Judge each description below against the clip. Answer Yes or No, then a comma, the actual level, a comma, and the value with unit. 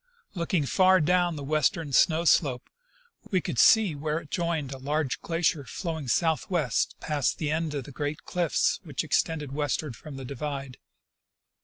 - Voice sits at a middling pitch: Yes, medium, 155 Hz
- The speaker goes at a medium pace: Yes, average, 160 wpm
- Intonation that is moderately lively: Yes, average, 3.1 semitones